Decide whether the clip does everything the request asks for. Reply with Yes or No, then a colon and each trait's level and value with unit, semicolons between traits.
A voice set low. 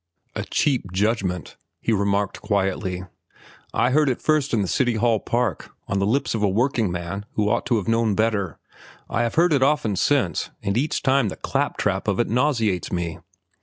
Yes: low, 110 Hz